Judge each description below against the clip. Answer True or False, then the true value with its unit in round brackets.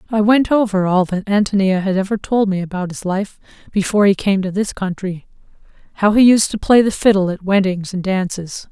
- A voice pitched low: False (195 Hz)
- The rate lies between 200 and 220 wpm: True (205 wpm)